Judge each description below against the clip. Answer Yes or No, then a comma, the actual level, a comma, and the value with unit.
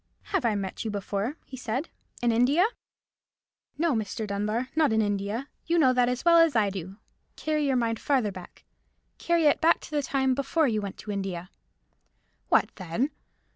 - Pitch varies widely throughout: Yes, wide, 6.1 semitones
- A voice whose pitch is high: Yes, high, 240 Hz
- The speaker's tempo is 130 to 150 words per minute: No, average, 180 wpm